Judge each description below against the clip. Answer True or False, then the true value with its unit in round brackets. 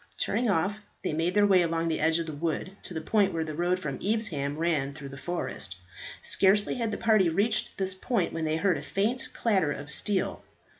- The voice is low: False (175 Hz)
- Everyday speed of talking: False (215 wpm)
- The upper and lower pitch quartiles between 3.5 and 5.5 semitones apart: True (4.4 semitones)